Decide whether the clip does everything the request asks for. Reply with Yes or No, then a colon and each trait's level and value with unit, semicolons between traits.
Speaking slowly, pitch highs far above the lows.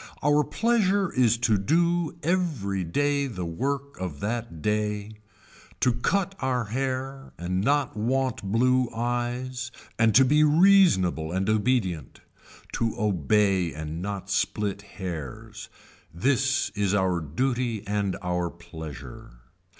Yes: slow, 120 wpm; wide, 6.1 semitones